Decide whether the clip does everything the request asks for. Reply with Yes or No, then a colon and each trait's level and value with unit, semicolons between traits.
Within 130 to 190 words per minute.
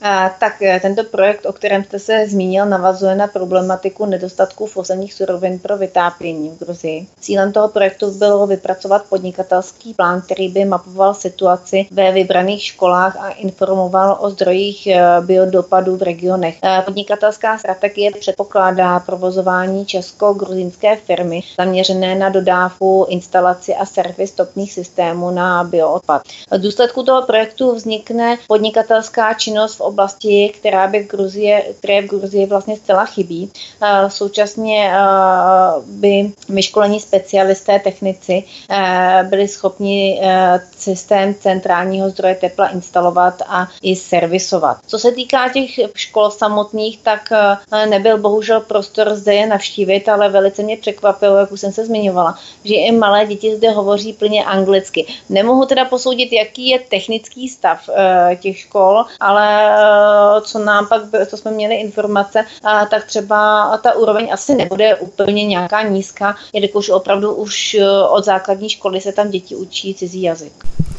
Yes: average, 135 wpm